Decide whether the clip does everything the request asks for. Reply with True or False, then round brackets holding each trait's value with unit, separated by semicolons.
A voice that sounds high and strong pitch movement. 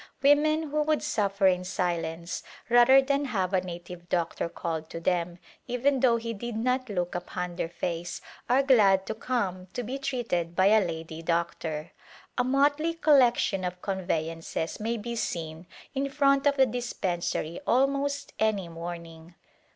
True (195 Hz; 7.1 semitones)